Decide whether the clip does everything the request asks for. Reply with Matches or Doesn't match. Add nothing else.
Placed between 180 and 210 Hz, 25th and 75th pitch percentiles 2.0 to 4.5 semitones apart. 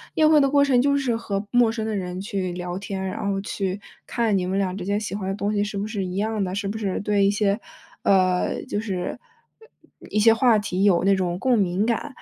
Matches